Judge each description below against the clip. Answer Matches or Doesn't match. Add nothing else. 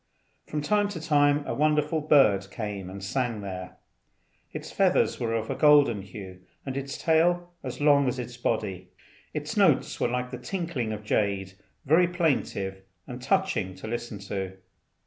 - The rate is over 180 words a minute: Doesn't match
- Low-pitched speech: Matches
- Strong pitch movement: Matches